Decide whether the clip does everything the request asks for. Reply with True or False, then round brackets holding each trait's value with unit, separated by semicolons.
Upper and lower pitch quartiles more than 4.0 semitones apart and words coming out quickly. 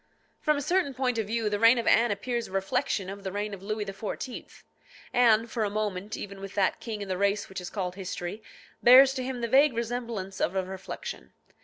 False (3.6 semitones; 220 wpm)